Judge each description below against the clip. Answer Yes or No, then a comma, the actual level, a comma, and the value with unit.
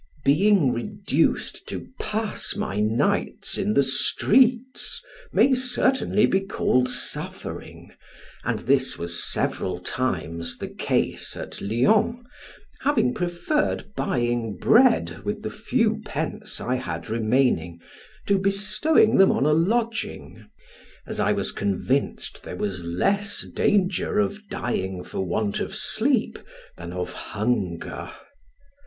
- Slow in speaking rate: Yes, slow, 120 wpm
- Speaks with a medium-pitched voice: Yes, medium, 160 Hz